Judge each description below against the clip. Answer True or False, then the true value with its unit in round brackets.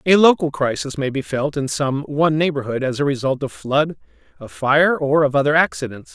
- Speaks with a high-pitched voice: False (140 Hz)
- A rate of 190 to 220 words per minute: True (205 wpm)